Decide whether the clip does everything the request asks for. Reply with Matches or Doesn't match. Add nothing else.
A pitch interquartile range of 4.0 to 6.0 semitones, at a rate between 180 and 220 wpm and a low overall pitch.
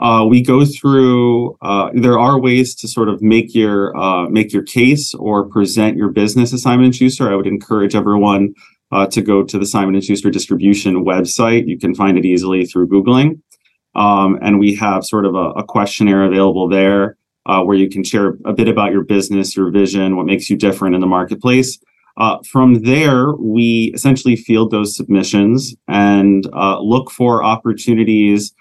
Doesn't match